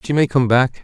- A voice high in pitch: No, low, 130 Hz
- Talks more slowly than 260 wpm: No, fast, 290 wpm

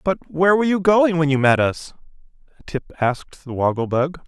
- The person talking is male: Yes, male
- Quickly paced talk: No, average, 195 wpm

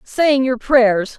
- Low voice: No, very high, 250 Hz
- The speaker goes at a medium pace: Yes, average, 150 wpm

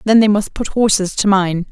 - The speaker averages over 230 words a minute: Yes, fast, 245 wpm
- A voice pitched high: Yes, high, 200 Hz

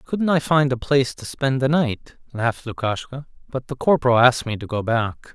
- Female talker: No, male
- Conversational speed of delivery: No, fast, 215 wpm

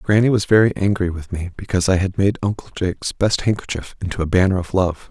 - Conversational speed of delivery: No, fast, 225 wpm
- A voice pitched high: No, very low, 95 Hz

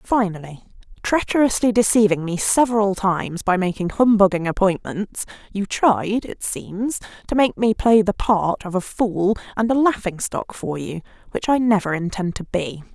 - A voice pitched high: Yes, high, 200 Hz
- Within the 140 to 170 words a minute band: Yes, average, 160 wpm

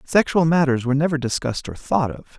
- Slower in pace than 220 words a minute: Yes, average, 200 wpm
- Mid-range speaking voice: Yes, medium, 145 Hz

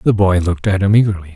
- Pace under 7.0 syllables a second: No, 7.4 syllables/s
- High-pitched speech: No, very low, 95 Hz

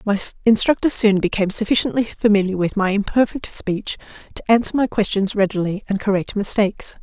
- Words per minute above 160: No, average, 155 wpm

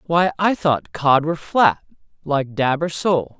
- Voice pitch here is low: No, medium, 150 Hz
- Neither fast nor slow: Yes, average, 175 wpm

